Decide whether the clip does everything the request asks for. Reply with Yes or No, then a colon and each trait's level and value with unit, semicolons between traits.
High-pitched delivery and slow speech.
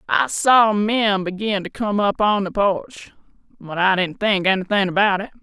No: high, 200 Hz; average, 175 wpm